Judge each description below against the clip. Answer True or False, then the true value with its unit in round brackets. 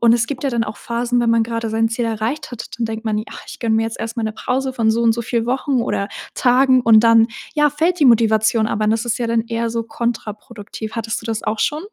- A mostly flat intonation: True (1.7 semitones)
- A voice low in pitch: False (230 Hz)